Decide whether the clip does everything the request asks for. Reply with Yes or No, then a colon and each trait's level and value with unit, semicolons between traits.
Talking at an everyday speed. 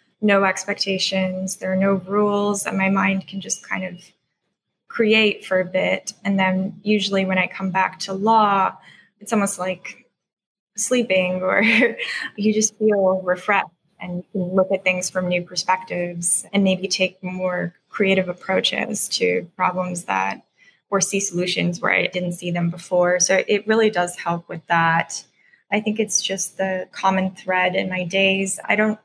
Yes: average, 165 wpm